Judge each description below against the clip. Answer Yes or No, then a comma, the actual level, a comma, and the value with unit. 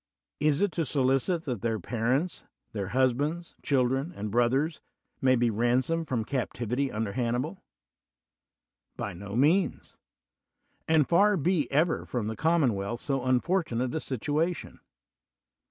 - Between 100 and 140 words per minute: Yes, slow, 135 wpm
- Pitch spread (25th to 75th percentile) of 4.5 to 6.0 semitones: Yes, average, 5.2 semitones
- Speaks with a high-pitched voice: No, low, 130 Hz